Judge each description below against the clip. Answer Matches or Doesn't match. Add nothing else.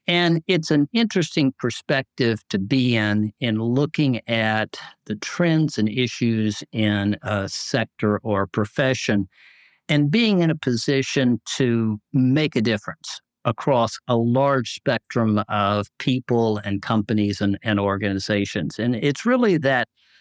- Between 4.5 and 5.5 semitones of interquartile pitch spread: Matches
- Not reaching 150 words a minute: Matches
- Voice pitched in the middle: Doesn't match